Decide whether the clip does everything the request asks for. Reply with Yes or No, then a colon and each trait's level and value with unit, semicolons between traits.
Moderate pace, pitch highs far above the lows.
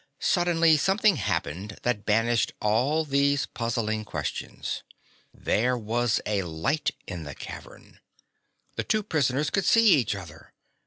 No: slow, 125 wpm; wide, 6.5 semitones